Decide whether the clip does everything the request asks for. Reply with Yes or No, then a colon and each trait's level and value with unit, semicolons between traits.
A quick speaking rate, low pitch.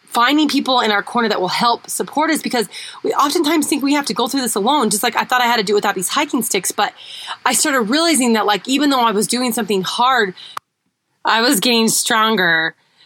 No: fast, 235 wpm; high, 240 Hz